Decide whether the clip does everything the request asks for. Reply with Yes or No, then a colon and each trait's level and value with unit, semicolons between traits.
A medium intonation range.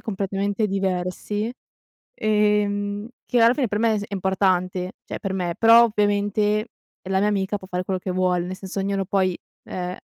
No: narrow, 2.0 semitones